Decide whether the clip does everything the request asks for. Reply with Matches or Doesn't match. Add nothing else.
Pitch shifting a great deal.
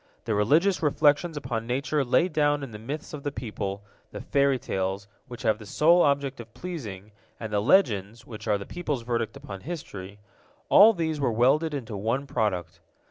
Matches